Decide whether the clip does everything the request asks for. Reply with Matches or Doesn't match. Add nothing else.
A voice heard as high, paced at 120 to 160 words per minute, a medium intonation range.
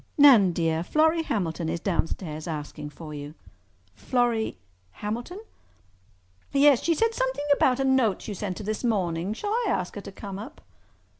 Doesn't match